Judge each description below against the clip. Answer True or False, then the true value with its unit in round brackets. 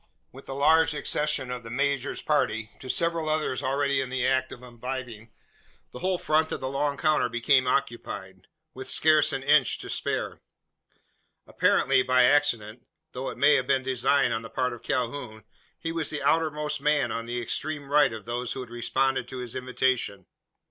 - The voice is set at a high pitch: False (130 Hz)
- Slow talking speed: False (185 wpm)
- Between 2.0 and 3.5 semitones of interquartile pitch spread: True (3.1 semitones)